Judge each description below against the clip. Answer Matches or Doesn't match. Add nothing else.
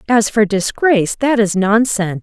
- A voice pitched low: Doesn't match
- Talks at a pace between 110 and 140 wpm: Matches